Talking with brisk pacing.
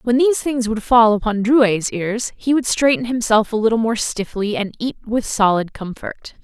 No: average, 195 wpm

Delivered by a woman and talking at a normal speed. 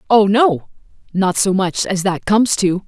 Yes: female; average, 190 wpm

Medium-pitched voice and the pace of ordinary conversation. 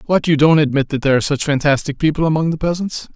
No: medium, 150 Hz; fast, 245 wpm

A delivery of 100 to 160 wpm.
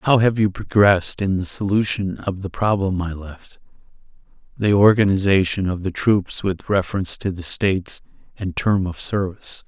Yes: average, 155 wpm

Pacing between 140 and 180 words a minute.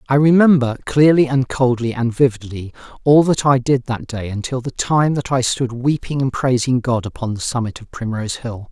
No: average, 200 wpm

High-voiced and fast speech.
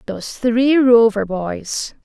No: high, 230 Hz; slow, 120 wpm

